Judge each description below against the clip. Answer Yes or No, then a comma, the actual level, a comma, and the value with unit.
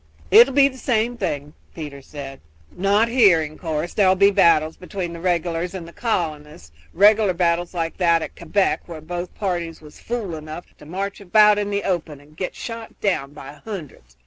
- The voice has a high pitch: No, medium, 175 Hz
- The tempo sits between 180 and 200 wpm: Yes, average, 195 wpm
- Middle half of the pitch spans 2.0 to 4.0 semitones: No, average, 4.5 semitones